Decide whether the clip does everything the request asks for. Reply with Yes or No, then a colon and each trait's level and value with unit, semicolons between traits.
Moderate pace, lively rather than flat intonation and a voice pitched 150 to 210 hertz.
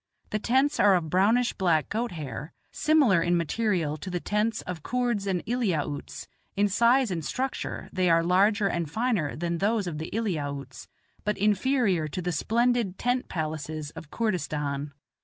Yes: average, 160 wpm; wide, 6.2 semitones; medium, 185 Hz